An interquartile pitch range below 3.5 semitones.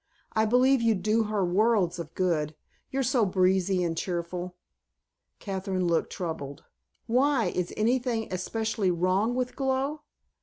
No: average, 4.6 semitones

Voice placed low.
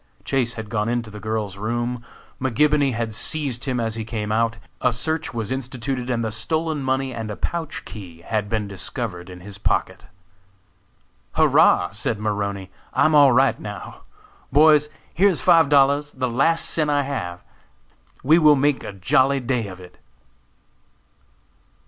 Yes: low, 120 Hz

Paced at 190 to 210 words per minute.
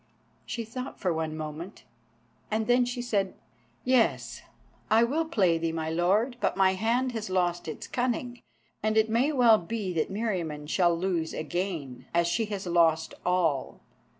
No: average, 160 wpm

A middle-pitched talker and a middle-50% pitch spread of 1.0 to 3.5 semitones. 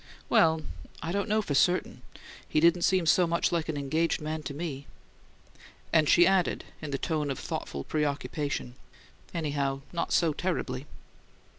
Yes: medium, 155 Hz; average, 3.0 semitones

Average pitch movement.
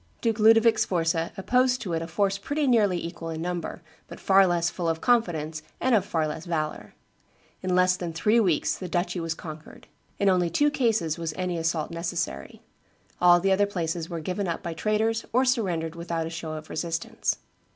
Yes: average, 3.8 semitones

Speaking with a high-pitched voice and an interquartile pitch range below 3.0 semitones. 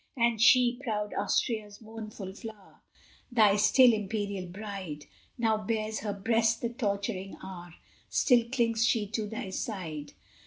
Yes: high, 215 Hz; narrow, 2.4 semitones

